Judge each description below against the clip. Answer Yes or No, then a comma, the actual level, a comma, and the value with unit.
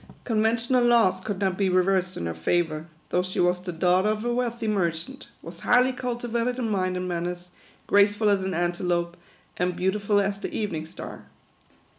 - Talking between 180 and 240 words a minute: Yes, average, 190 wpm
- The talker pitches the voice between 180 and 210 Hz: Yes, high, 190 Hz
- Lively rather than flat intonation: No, average, 3.8 semitones